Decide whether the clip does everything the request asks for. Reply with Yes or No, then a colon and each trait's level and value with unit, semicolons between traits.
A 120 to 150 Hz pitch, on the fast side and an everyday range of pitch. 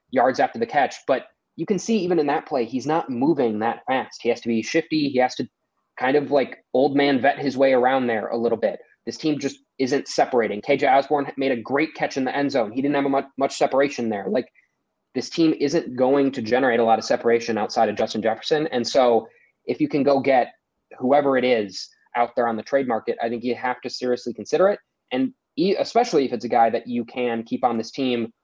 Yes: low, 135 Hz; fast, 240 wpm; average, 3.5 semitones